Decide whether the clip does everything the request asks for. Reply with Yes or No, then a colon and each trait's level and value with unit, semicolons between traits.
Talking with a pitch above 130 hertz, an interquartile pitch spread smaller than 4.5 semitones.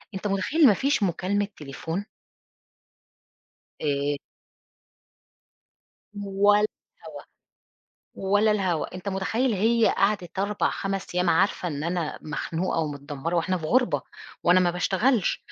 Yes: high, 190 Hz; average, 3.5 semitones